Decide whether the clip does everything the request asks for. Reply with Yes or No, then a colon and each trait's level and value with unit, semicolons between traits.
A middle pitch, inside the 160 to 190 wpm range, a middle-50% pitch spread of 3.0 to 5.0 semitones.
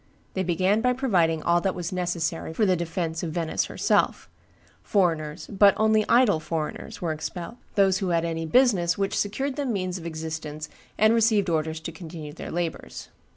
Yes: medium, 175 Hz; average, 170 wpm; average, 3.9 semitones